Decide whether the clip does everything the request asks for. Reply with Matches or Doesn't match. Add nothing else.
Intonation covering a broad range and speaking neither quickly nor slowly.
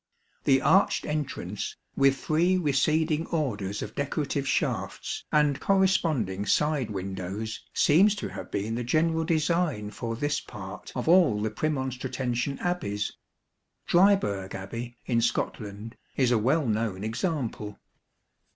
Doesn't match